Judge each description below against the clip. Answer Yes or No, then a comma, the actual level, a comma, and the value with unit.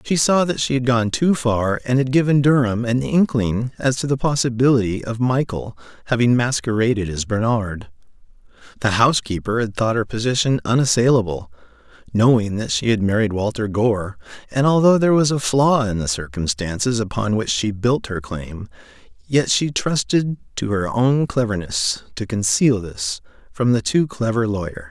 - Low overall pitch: Yes, low, 115 Hz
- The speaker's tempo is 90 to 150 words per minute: No, average, 165 wpm